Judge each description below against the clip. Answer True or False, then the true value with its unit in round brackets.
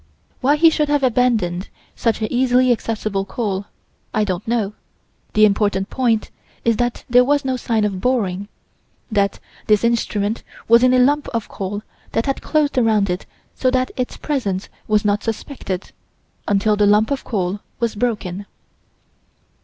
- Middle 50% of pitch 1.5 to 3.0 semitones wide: False (3.7 semitones)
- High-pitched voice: True (220 Hz)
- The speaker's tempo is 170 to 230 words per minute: False (155 wpm)